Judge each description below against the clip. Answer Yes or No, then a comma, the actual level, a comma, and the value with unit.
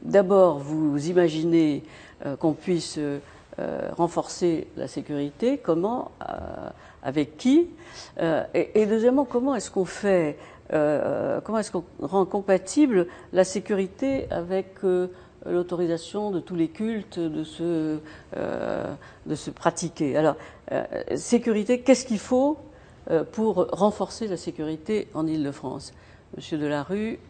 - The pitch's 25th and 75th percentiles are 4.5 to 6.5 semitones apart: Yes, wide, 5.4 semitones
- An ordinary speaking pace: No, slow, 125 wpm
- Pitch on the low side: No, medium, 180 Hz